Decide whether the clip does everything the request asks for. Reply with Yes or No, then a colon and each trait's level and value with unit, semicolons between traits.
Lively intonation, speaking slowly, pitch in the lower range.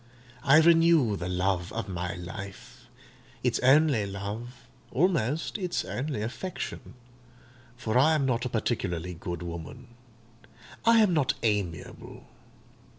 Yes: wide, 6.6 semitones; slow, 110 wpm; low, 120 Hz